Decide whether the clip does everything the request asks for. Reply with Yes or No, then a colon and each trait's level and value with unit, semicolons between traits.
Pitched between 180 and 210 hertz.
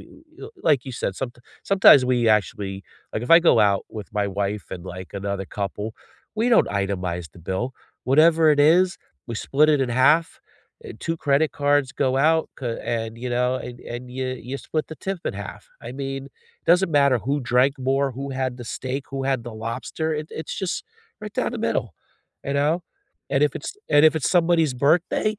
No: low, 135 Hz